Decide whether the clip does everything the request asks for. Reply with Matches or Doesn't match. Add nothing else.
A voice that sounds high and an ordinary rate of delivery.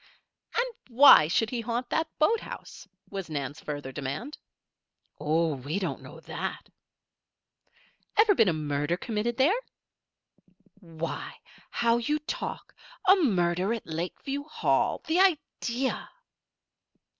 Doesn't match